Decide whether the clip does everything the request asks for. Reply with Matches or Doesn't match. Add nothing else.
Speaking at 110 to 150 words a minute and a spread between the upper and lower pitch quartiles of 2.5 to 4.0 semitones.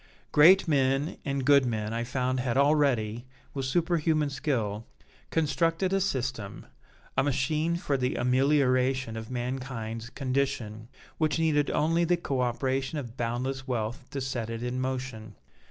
Matches